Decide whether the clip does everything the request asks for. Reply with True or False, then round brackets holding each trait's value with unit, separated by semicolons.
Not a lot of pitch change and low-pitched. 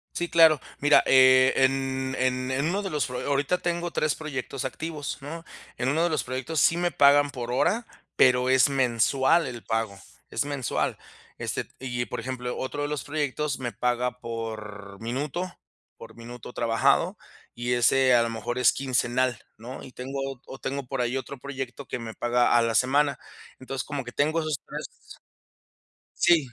False (3.0 semitones; 130 Hz)